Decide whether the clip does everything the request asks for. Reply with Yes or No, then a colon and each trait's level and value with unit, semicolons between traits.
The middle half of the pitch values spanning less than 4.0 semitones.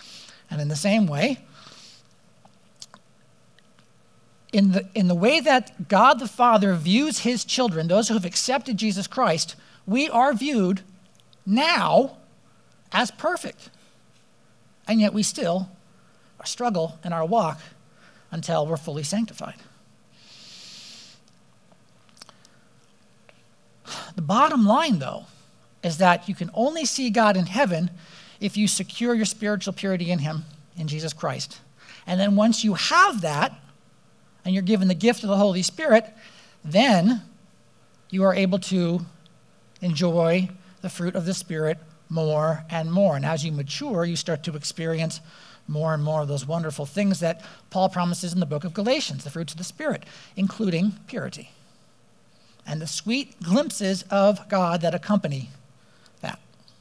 No: average, 4.6 semitones